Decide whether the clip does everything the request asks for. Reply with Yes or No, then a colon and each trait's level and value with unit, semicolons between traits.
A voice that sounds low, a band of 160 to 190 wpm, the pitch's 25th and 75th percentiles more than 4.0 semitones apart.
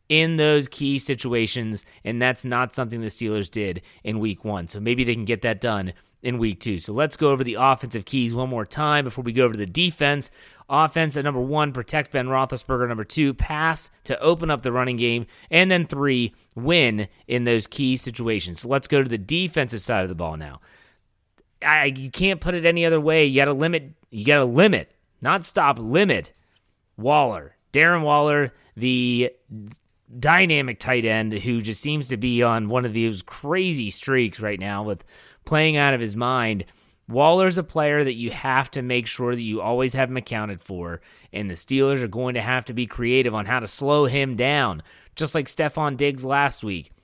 No: low, 125 Hz; fast, 205 wpm; average, 4.7 semitones